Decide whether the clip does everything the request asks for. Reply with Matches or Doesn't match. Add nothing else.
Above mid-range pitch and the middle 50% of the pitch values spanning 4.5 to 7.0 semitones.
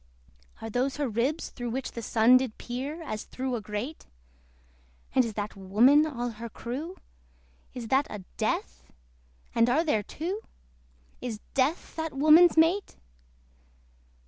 Matches